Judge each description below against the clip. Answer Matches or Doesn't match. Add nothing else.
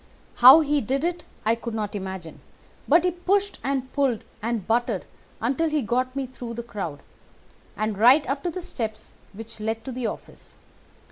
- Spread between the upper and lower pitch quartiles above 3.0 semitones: Matches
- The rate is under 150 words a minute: Doesn't match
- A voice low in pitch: Doesn't match